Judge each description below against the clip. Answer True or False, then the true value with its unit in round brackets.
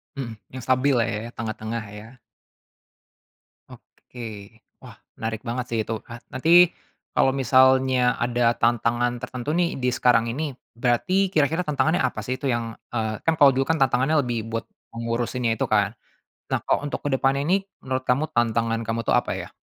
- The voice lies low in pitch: True (120 Hz)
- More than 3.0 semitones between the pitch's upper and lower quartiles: False (2.4 semitones)